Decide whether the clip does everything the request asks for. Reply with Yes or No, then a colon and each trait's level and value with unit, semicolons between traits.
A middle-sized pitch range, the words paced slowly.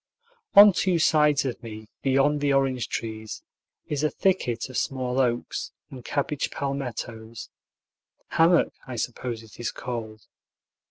Yes: average, 3.8 semitones; slow, 130 wpm